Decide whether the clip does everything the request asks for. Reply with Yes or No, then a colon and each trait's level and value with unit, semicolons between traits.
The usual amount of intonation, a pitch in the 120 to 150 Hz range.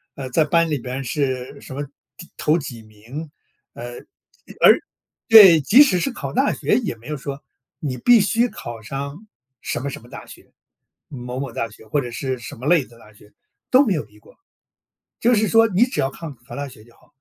No: wide, 6.4 semitones; medium, 140 Hz